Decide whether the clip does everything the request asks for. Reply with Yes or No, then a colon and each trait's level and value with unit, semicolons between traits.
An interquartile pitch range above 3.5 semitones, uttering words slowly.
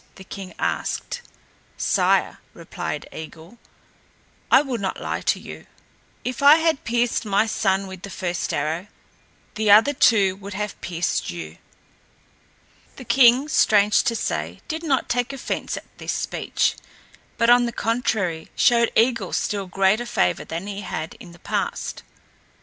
No: average, 4.4 semitones; average, 150 wpm